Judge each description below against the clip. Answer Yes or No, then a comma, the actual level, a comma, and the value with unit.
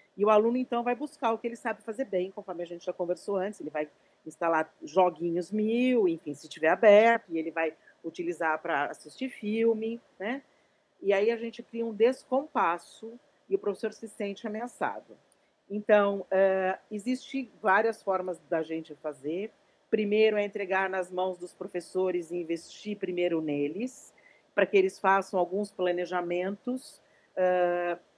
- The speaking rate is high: No, average, 160 wpm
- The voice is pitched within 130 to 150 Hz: No, high, 195 Hz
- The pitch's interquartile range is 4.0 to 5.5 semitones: Yes, average, 4.4 semitones